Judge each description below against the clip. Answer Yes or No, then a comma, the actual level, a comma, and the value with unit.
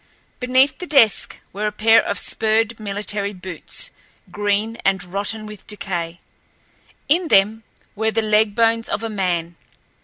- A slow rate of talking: No, average, 145 wpm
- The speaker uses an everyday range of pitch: No, narrow, 2.3 semitones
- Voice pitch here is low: No, high, 210 Hz